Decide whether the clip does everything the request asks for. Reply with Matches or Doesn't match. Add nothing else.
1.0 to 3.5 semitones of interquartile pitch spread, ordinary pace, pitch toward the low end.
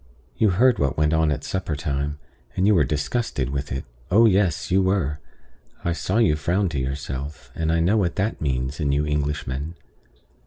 Doesn't match